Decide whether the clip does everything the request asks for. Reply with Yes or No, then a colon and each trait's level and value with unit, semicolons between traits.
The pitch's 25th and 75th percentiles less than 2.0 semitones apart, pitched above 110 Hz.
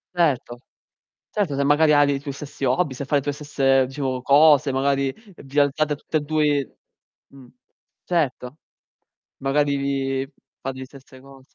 Yes: narrow, 1.6 semitones; medium, 140 Hz